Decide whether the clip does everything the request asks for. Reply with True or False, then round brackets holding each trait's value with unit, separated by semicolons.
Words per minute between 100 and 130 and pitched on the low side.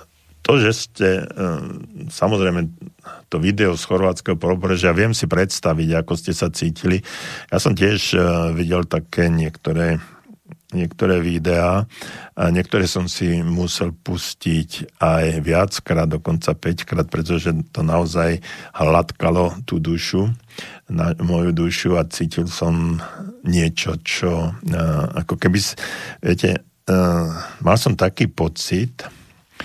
True (110 wpm; 85 Hz)